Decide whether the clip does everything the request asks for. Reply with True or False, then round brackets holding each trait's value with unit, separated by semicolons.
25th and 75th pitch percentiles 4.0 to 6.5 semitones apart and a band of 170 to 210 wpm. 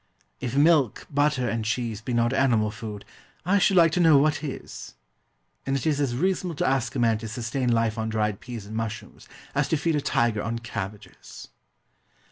True (4.6 semitones; 195 wpm)